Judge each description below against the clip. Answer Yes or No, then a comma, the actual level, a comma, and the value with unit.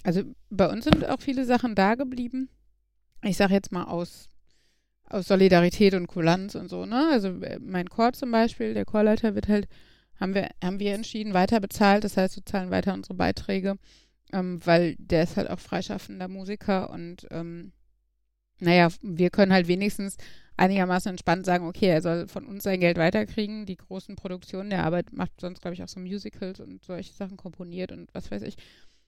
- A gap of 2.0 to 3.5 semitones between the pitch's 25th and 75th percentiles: Yes, average, 2.8 semitones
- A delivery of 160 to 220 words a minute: Yes, average, 185 wpm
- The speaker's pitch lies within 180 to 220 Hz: Yes, high, 190 Hz